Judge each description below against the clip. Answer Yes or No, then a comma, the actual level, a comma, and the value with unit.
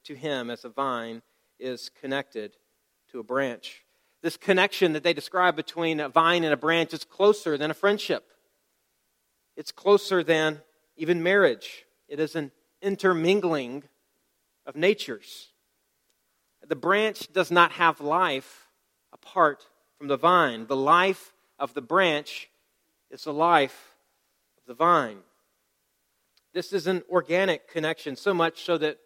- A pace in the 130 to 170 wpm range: Yes, average, 140 wpm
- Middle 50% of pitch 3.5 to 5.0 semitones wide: Yes, average, 3.9 semitones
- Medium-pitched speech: Yes, medium, 165 Hz